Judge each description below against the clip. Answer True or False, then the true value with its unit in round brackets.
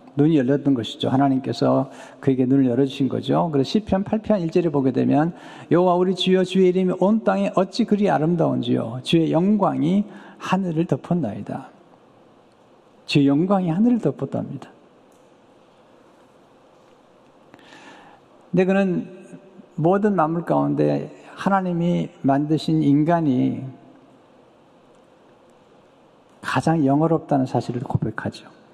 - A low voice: False (160 Hz)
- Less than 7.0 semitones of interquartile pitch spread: True (5.4 semitones)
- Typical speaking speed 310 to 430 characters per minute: False (250 characters per minute)